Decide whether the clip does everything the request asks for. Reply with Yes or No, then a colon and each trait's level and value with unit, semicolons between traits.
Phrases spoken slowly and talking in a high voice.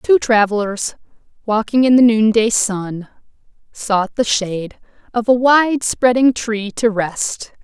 Yes: slow, 125 wpm; high, 225 Hz